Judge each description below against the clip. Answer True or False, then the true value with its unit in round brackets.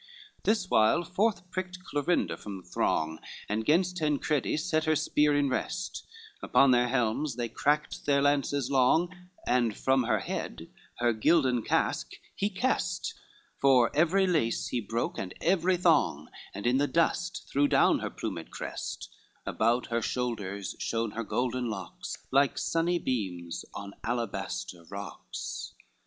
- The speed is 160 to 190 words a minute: False (145 wpm)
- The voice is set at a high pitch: False (135 Hz)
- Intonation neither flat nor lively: False (6.1 semitones)